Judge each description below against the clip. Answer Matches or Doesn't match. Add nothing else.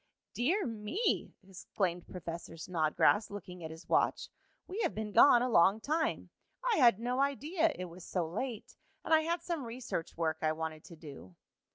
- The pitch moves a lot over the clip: Matches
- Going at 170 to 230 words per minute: Matches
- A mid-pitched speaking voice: Doesn't match